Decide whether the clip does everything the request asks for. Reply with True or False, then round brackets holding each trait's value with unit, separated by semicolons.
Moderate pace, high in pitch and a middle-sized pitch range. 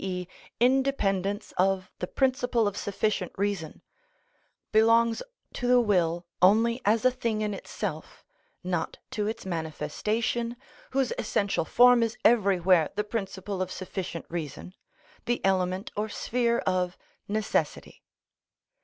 False (120 wpm; 205 Hz; 4.0 semitones)